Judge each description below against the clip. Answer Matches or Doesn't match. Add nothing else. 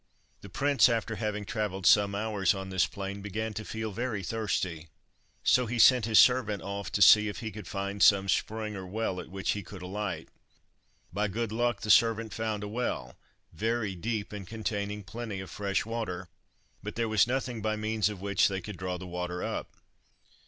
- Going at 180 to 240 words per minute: Matches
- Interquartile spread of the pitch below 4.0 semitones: Matches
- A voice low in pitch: Matches